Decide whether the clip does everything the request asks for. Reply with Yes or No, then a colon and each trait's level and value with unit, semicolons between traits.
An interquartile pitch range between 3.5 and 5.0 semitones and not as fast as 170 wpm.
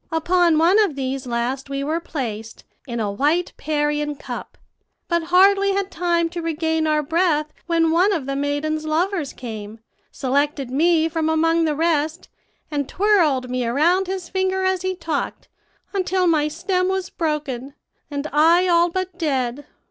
Yes: average, 3.8 semitones; average, 160 wpm